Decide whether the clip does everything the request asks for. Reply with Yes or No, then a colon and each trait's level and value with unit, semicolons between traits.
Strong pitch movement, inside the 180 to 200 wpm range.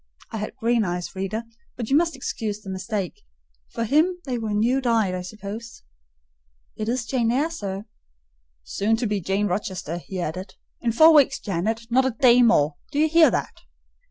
No: average, 4.8 semitones; average, 185 wpm